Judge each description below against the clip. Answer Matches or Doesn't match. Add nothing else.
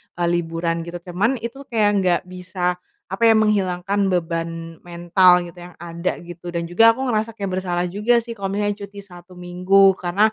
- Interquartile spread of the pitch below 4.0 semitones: Matches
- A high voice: Doesn't match